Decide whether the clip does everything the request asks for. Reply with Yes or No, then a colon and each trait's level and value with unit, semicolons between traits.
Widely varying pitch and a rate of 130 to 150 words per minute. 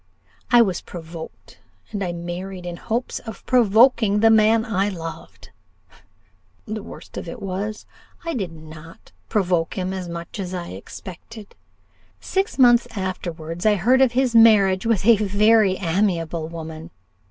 No: average, 4.5 semitones; average, 145 wpm